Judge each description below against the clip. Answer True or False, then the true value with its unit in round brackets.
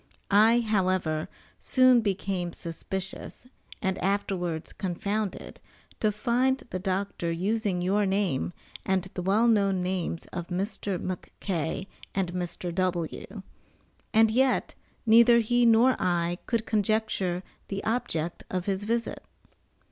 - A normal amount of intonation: True (3.6 semitones)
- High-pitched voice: True (195 Hz)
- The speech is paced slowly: True (120 wpm)